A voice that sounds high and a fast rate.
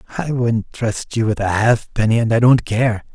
No: low, 115 Hz; fast, 210 wpm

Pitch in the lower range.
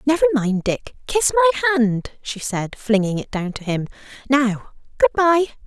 No: very high, 250 Hz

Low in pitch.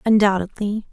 No: high, 205 Hz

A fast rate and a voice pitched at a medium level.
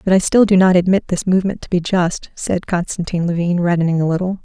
Yes: fast, 230 wpm; medium, 180 Hz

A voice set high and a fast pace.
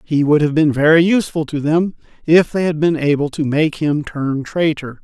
No: medium, 155 Hz; fast, 215 wpm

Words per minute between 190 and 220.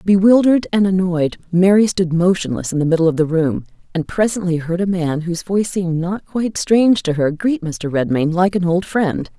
Yes: fast, 205 wpm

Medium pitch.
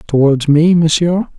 Yes: medium, 160 Hz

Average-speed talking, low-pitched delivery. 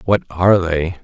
Yes: average, 175 wpm; very low, 90 Hz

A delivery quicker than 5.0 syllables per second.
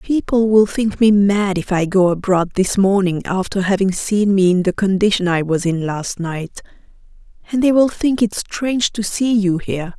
No: 4.7 syllables/s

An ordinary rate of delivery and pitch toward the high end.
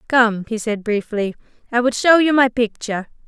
Yes: average, 185 wpm; high, 235 Hz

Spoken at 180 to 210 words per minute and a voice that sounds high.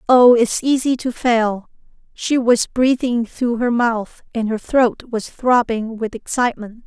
No: average, 155 wpm; high, 235 Hz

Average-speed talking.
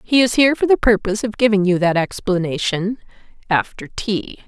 Yes: average, 160 wpm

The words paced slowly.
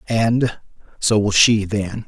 Yes: slow, 115 wpm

